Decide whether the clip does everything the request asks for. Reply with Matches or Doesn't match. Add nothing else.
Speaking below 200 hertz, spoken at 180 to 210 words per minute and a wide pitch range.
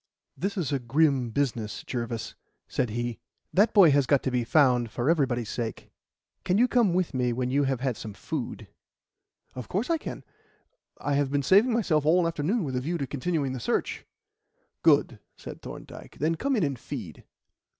Matches